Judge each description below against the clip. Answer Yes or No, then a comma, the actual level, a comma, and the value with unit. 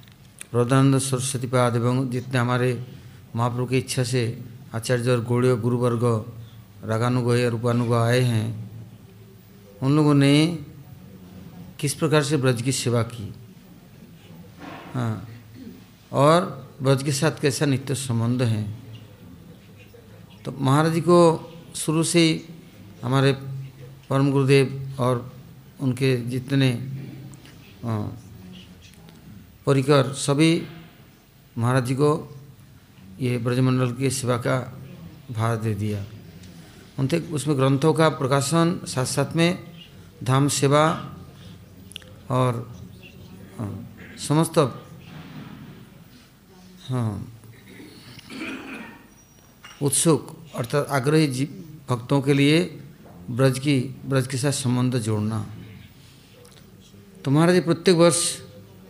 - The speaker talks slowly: Yes, slow, 100 wpm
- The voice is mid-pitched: No, low, 130 Hz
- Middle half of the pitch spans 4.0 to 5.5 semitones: No, average, 3.5 semitones